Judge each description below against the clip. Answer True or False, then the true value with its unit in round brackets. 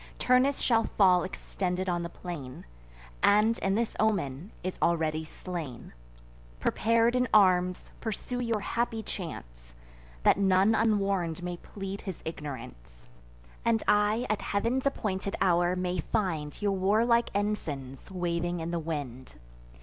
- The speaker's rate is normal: False (130 wpm)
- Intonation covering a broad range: False (4.6 semitones)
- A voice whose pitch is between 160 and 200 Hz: True (185 Hz)